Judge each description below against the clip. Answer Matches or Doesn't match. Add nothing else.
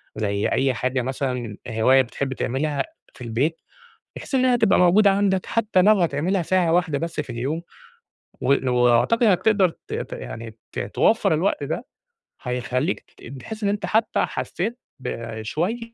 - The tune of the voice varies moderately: Doesn't match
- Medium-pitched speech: Matches